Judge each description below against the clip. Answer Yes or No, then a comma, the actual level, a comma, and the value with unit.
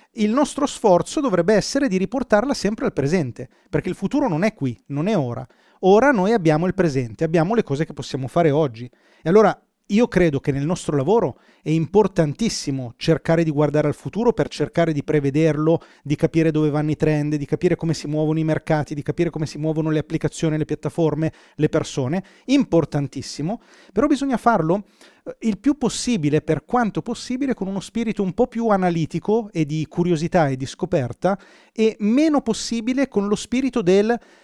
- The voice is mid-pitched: Yes, medium, 170 Hz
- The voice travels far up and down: Yes, wide, 6.2 semitones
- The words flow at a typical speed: No, fast, 180 wpm